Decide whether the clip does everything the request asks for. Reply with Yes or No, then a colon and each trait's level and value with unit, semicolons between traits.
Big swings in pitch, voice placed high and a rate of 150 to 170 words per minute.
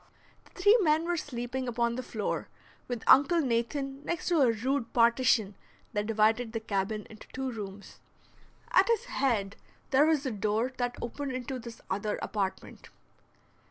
No: average, 3.8 semitones; high, 245 Hz; average, 160 wpm